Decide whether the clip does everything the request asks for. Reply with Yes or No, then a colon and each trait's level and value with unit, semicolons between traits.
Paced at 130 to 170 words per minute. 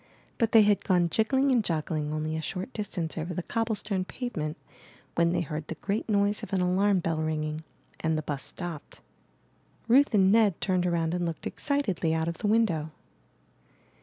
No: average, 190 wpm